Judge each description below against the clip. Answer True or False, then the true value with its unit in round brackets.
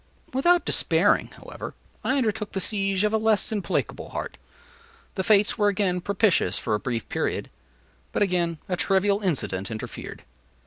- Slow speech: False (150 wpm)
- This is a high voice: True (195 Hz)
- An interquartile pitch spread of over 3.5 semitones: False (3.1 semitones)